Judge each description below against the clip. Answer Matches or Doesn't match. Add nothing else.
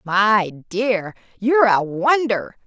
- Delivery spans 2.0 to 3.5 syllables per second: Matches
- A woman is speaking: Matches